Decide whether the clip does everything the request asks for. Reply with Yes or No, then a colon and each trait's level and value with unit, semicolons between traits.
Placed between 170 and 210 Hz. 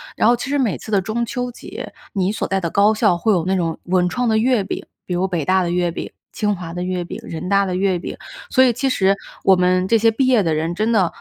Yes: high, 190 Hz